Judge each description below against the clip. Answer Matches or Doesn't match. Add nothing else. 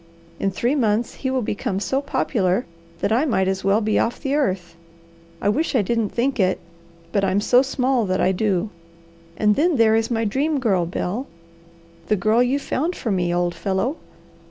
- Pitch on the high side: Matches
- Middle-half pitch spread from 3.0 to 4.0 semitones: Doesn't match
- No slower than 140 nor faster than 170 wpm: Doesn't match